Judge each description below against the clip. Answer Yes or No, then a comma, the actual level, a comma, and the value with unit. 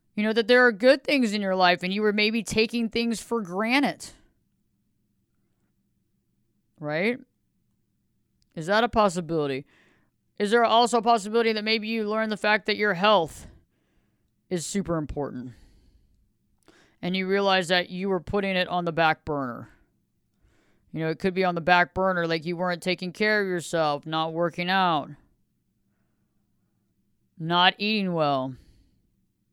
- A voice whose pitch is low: No, medium, 180 Hz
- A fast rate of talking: No, average, 150 wpm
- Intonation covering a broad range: Yes, wide, 7.6 semitones